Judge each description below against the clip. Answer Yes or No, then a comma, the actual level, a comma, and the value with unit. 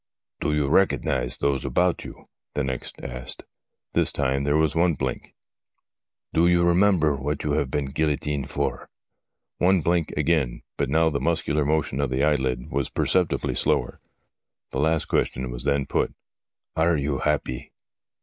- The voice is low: Yes, very low, 75 Hz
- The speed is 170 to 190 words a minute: Yes, average, 175 wpm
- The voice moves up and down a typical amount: Yes, average, 3.0 semitones